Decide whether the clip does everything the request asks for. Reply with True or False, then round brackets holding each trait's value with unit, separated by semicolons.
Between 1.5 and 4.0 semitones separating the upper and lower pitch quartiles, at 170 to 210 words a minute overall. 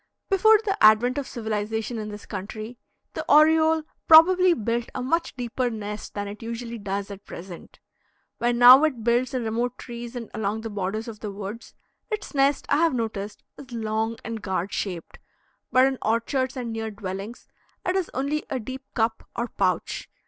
True (3.6 semitones; 180 wpm)